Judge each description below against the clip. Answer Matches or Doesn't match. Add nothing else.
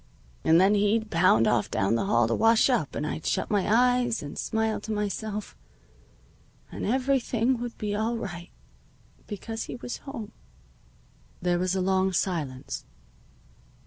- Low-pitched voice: Doesn't match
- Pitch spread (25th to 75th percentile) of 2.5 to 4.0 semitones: Doesn't match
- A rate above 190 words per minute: Doesn't match